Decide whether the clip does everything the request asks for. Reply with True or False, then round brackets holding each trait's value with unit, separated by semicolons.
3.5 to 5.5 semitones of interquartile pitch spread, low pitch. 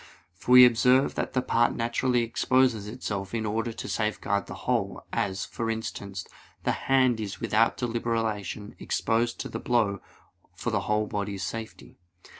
False (2.6 semitones; 115 Hz)